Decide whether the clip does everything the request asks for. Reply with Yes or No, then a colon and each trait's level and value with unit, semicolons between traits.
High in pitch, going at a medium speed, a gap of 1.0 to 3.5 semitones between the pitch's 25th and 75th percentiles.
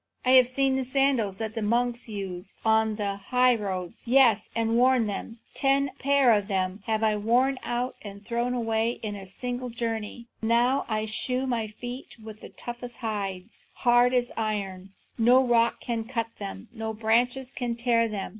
Yes: high, 230 Hz; average, 175 wpm; average, 2.7 semitones